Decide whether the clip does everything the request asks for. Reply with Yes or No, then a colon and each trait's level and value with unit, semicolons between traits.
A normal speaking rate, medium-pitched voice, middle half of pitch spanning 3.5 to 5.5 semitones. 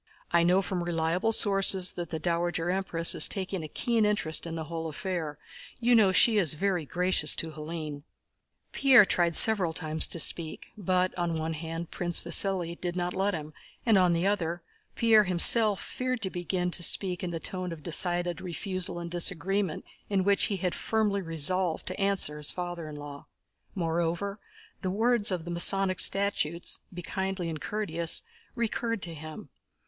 No: average, 175 wpm; medium, 180 Hz; average, 2.9 semitones